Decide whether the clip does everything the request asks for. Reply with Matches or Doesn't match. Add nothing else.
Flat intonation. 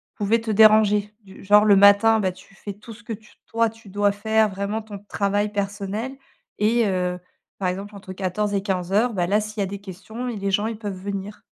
Matches